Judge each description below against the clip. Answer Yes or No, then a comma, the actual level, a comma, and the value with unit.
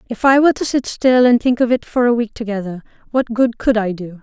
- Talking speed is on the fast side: Yes, fast, 270 wpm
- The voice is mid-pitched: No, high, 235 Hz